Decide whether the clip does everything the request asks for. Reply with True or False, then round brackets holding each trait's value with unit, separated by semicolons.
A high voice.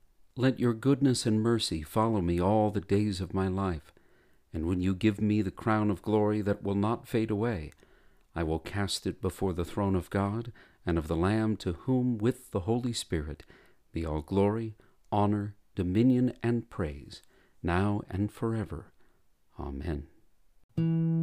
False (100 Hz)